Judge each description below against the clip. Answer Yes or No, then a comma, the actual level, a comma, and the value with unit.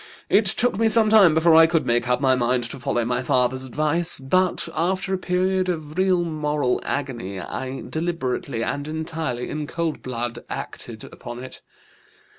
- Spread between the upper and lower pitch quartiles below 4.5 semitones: No, wide, 5.5 semitones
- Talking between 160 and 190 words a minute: Yes, average, 170 wpm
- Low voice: No, medium, 155 Hz